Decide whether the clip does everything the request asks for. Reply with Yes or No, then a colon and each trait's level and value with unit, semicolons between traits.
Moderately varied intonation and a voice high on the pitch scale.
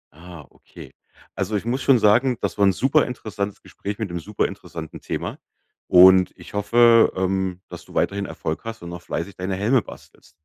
No: average, 4.0 semitones; low, 100 Hz